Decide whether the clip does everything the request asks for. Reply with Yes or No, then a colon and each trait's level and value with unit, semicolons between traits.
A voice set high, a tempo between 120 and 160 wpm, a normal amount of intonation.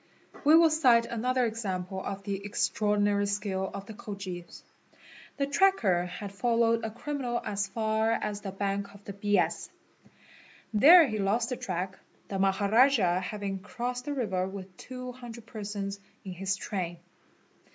Yes: high, 205 Hz; average, 150 wpm; average, 3.5 semitones